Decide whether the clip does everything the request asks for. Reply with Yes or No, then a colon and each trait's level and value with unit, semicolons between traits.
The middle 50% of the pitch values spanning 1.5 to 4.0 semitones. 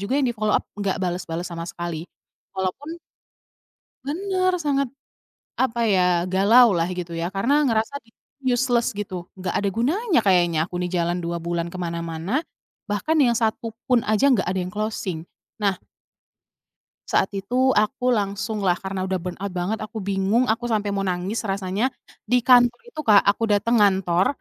No: average, 4.6 semitones